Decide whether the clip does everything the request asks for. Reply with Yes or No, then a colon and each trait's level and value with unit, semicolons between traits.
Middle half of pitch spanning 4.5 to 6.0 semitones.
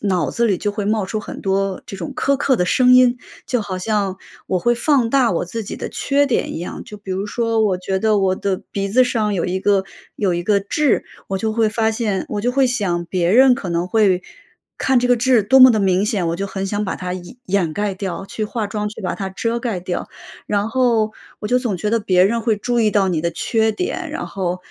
No: average, 3.6 semitones